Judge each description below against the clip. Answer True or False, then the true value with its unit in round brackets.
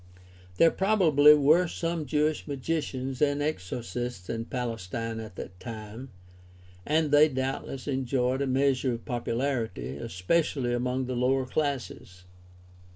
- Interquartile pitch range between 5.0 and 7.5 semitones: False (3.8 semitones)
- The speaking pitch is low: True (130 Hz)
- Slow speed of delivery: True (120 wpm)